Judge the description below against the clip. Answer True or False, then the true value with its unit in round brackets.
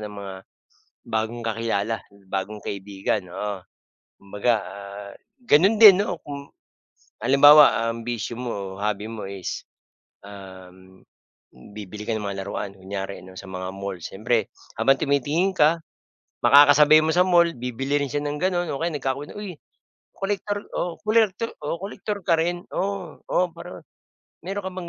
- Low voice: True (125 Hz)